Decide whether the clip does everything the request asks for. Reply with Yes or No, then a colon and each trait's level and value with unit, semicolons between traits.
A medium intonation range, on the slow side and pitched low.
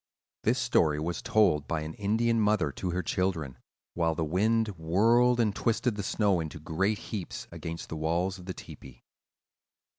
No: average, 5.0 semitones; average, 170 wpm; very low, 90 Hz